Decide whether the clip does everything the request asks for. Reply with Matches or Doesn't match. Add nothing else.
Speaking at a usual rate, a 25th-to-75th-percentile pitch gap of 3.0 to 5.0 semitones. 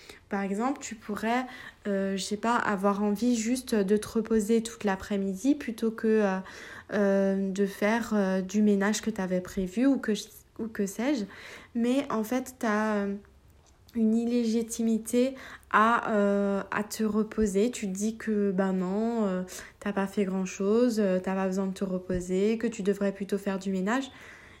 Doesn't match